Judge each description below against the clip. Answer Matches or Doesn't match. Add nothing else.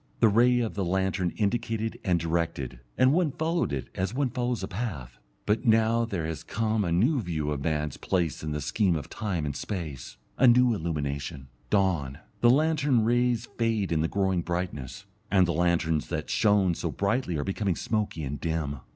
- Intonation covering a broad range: Matches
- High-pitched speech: Doesn't match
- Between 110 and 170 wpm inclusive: Doesn't match